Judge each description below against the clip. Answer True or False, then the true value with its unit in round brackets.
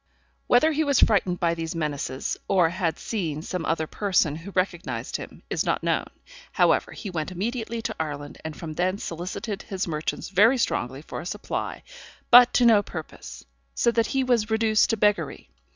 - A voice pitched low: False (190 Hz)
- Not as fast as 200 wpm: True (180 wpm)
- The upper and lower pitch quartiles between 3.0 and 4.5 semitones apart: False (5.6 semitones)